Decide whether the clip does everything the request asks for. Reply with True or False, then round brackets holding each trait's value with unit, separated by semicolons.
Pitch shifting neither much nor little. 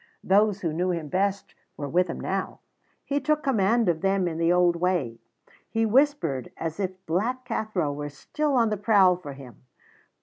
True (4.7 semitones)